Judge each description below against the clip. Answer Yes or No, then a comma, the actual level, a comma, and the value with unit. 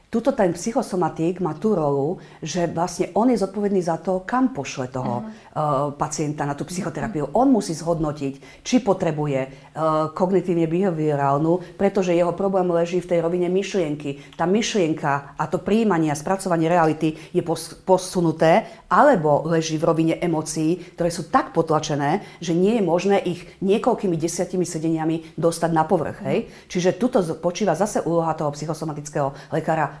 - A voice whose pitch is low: No, medium, 170 Hz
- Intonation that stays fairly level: No, average, 3.0 semitones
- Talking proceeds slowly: No, average, 150 wpm